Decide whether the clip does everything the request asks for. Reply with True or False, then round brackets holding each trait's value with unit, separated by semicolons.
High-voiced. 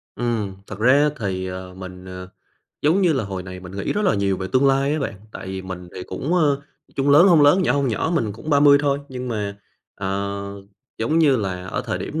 False (110 Hz)